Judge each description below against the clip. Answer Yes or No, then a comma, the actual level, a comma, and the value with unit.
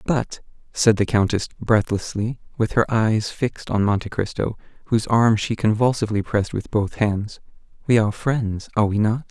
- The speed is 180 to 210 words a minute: No, average, 170 wpm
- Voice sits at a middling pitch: No, low, 110 Hz